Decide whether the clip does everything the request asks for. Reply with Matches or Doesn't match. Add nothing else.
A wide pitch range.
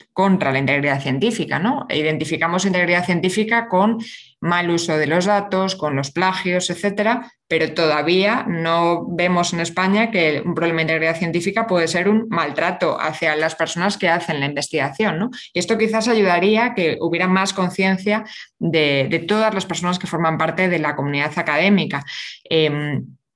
Doesn't match